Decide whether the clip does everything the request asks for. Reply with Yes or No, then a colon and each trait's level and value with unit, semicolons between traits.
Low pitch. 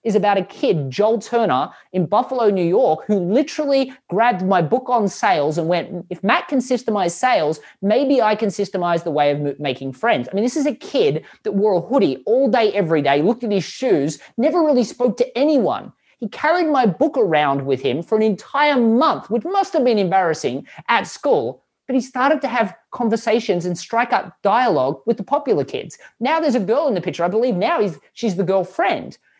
No: high, 220 Hz